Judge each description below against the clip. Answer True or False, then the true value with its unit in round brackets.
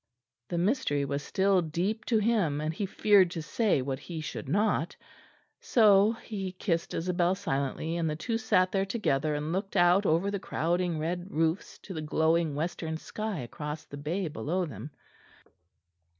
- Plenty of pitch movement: False (4.2 semitones)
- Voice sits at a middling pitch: True (175 Hz)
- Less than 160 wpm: False (165 wpm)